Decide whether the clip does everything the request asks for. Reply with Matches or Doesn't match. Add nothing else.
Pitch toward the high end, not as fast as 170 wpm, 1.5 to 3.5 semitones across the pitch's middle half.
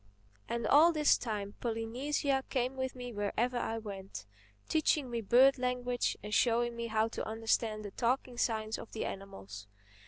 Matches